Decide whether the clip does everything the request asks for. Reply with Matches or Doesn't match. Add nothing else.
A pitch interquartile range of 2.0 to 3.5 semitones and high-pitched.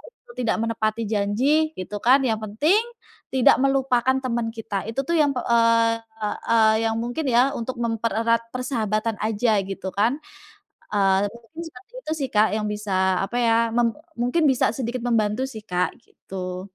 Matches